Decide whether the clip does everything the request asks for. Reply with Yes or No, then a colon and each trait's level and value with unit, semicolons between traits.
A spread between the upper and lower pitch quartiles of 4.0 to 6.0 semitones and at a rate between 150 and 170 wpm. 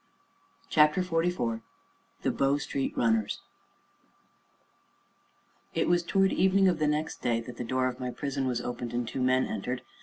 Yes: average, 5.1 semitones; average, 155 wpm